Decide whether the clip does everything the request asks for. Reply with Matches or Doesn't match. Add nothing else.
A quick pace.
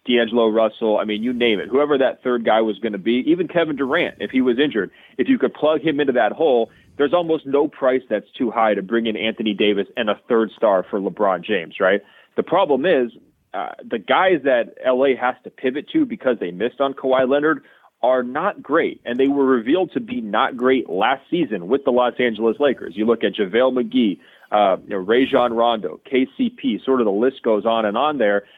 Matches